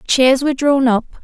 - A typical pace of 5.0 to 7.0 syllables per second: No, 4.8 syllables/s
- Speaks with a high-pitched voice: Yes, very high, 265 Hz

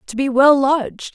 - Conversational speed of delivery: No, fast, 210 wpm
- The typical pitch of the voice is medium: No, very high, 270 Hz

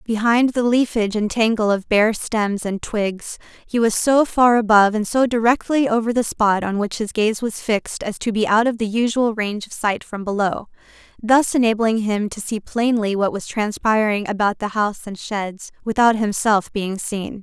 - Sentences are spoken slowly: No, average, 195 wpm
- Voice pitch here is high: Yes, high, 220 Hz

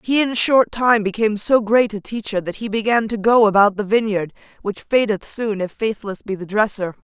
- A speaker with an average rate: No, fast, 210 wpm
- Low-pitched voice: No, high, 215 Hz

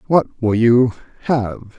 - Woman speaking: No, male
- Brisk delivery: No, slow, 135 wpm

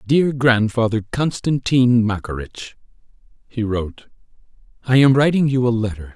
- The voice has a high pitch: No, low, 120 Hz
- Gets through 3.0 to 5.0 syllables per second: Yes, 4.7 syllables/s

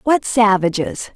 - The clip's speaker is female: Yes, female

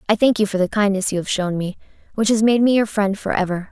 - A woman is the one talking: Yes, female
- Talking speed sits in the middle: No, fast, 290 wpm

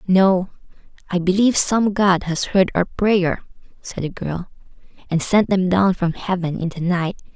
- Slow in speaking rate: No, average, 170 wpm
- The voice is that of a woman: Yes, female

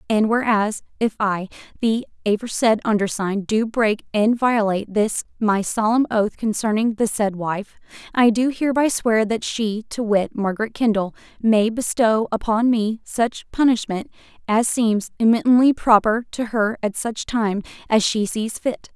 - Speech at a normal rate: Yes, average, 150 wpm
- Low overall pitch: No, high, 220 Hz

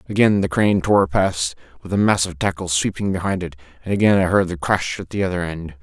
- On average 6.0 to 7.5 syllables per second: Yes, 6.1 syllables/s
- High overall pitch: No, very low, 90 Hz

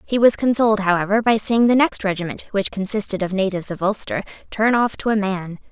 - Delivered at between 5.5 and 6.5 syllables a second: Yes, 6.0 syllables/s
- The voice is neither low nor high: No, high, 205 Hz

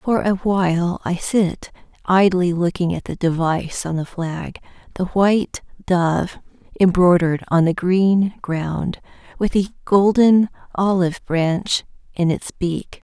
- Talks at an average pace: No, slow, 130 wpm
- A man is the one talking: No, female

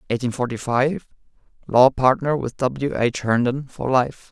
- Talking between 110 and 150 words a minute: Yes, average, 140 wpm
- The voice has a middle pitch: No, low, 130 Hz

